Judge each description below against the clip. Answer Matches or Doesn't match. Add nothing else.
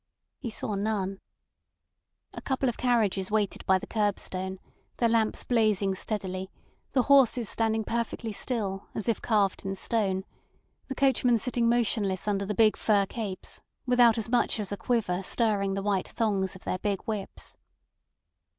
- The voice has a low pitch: Doesn't match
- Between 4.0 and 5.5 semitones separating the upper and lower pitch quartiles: Doesn't match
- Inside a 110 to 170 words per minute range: Matches